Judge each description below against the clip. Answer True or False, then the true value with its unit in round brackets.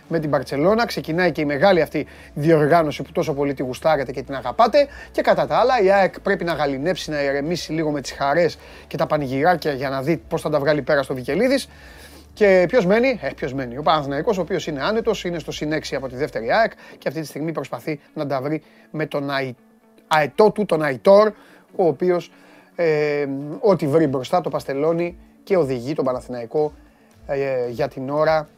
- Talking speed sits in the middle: False (200 wpm)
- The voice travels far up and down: False (3.6 semitones)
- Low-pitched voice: False (155 Hz)